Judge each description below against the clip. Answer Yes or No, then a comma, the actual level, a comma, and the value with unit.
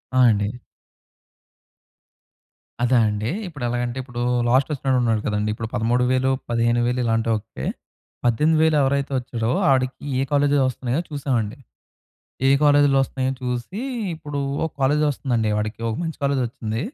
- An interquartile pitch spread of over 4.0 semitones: No, average, 3.5 semitones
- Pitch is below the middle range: Yes, low, 125 Hz